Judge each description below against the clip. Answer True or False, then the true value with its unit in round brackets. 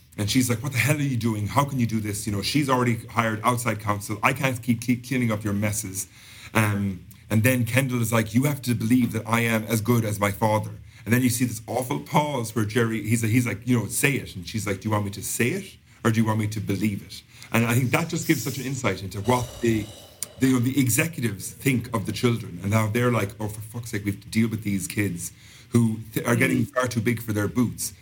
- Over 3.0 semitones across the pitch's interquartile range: False (2.7 semitones)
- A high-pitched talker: False (115 Hz)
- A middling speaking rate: False (270 wpm)